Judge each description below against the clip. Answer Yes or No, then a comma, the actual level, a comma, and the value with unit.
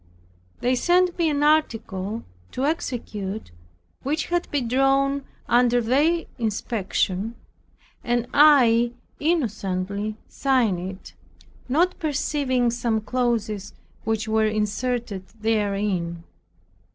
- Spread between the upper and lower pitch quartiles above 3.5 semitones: Yes, average, 4.7 semitones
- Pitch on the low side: No, high, 235 Hz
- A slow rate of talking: Yes, slow, 95 wpm